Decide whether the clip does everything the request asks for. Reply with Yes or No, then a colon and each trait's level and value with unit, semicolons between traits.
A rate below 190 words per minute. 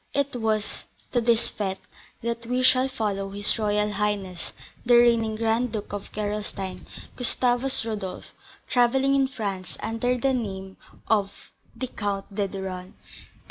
Yes: average, 140 wpm